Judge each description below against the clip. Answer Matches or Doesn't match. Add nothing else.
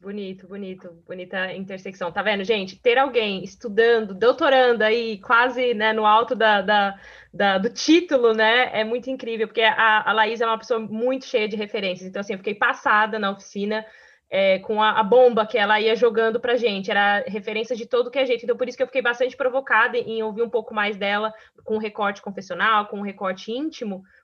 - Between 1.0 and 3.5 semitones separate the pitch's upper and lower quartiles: Matches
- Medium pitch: Doesn't match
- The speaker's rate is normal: Doesn't match